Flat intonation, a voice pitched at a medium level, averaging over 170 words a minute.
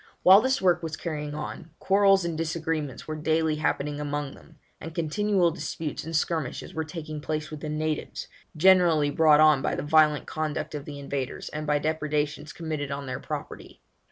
Yes: narrow, 1.7 semitones; medium, 155 Hz; average, 180 wpm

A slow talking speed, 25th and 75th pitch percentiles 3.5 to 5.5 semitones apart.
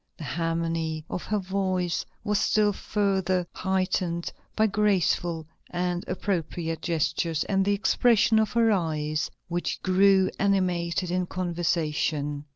No: slow, 120 wpm; average, 3.0 semitones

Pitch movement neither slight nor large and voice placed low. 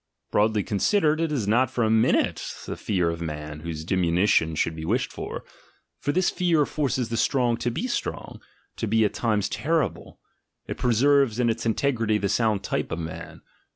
No: wide, 5.8 semitones; low, 110 Hz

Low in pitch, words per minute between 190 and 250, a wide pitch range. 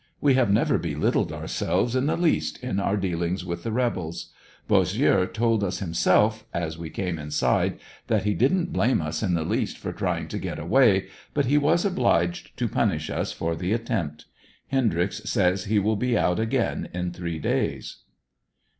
No: low, 100 Hz; average, 180 wpm; wide, 5.7 semitones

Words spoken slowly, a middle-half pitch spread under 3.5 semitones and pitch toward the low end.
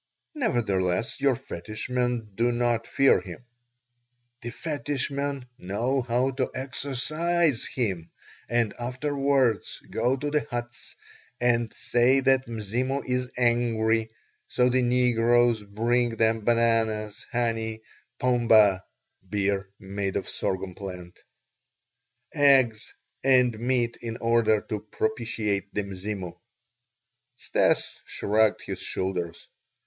Yes: slow, 110 wpm; average, 3.0 semitones; low, 120 Hz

